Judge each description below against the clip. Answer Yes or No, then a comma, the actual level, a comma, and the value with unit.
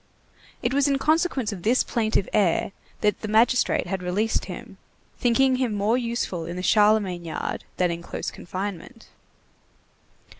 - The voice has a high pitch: Yes, high, 215 Hz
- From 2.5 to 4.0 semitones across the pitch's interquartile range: No, average, 4.8 semitones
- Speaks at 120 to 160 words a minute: Yes, average, 150 wpm